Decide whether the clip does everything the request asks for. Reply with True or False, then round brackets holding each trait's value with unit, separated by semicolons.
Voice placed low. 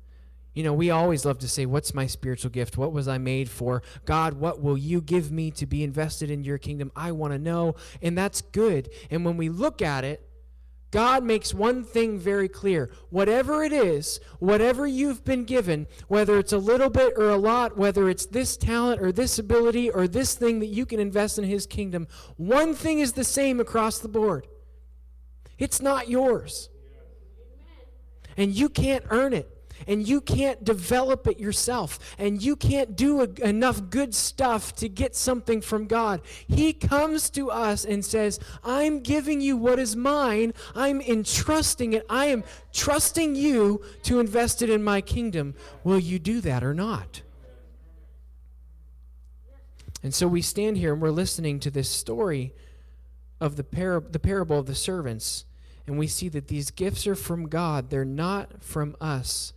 False (190 Hz)